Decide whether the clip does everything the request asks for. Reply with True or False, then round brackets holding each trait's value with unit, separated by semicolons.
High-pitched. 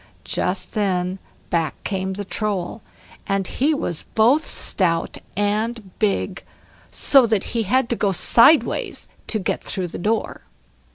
True (205 Hz)